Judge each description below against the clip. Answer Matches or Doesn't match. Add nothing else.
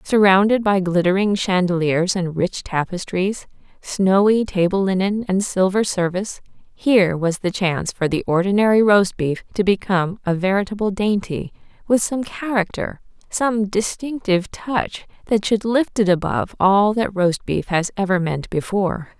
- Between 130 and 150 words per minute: Matches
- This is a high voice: Matches